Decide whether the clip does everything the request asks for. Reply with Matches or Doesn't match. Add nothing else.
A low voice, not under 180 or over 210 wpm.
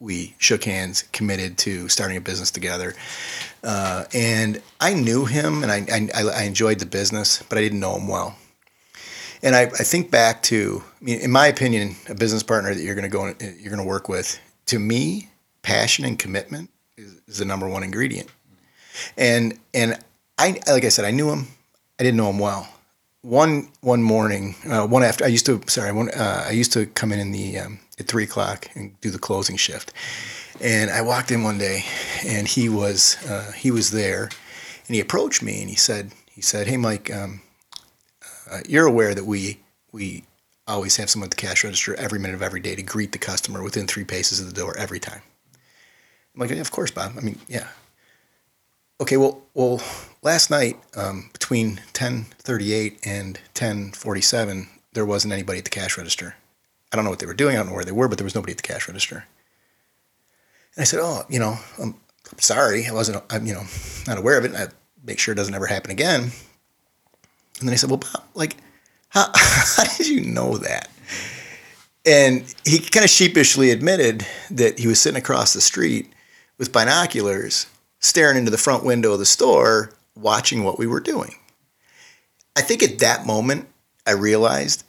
Matches